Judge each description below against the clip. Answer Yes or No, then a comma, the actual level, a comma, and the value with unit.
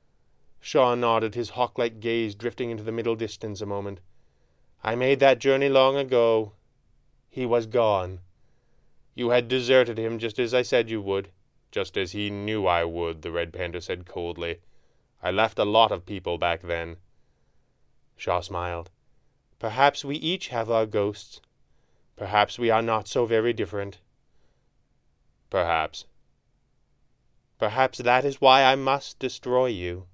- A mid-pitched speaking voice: No, low, 115 Hz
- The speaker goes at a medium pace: Yes, average, 145 wpm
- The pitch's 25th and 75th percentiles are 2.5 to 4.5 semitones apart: Yes, average, 4.0 semitones